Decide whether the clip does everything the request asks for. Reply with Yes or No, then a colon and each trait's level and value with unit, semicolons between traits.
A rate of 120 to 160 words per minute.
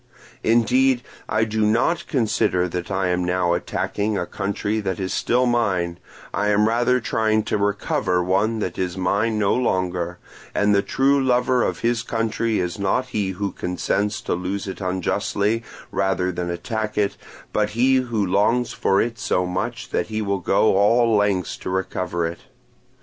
No: average, 170 wpm